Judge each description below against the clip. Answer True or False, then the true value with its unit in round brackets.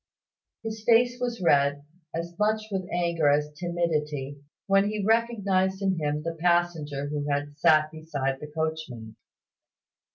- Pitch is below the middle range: False (165 Hz)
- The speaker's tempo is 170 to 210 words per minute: False (135 wpm)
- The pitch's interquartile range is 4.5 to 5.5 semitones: True (4.8 semitones)